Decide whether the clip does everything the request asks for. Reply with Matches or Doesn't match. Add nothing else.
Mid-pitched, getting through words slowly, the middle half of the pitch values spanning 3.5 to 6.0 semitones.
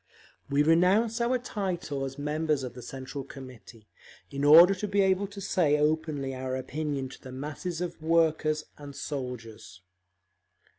Doesn't match